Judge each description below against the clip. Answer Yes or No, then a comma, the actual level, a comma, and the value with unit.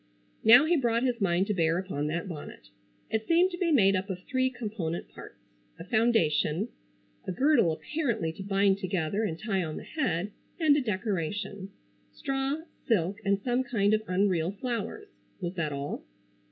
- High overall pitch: Yes, high, 200 Hz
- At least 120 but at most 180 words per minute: Yes, average, 165 wpm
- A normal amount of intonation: No, wide, 6.0 semitones